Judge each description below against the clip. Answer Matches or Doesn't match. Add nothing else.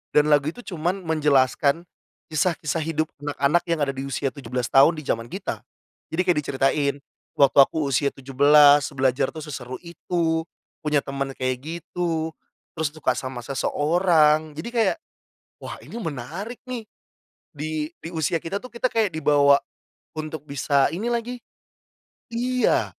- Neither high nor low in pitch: Matches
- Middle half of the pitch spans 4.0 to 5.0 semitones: Doesn't match